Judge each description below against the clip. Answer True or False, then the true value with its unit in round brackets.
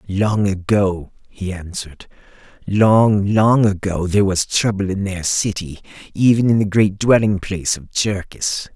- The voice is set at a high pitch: False (100 Hz)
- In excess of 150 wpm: False (145 wpm)